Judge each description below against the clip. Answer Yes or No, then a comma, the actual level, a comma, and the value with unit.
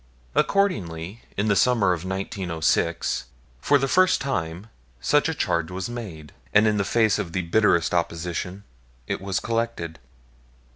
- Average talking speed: Yes, average, 145 wpm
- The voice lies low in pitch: Yes, very low, 95 Hz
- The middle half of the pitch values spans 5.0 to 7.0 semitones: Yes, average, 5.3 semitones